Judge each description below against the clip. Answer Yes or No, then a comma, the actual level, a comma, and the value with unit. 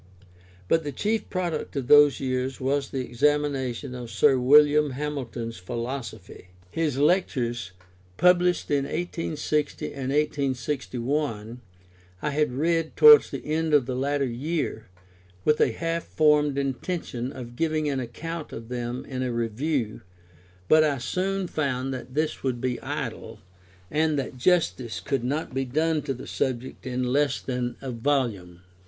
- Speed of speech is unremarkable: Yes, average, 145 wpm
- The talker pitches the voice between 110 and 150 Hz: Yes, low, 135 Hz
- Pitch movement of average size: Yes, average, 3.5 semitones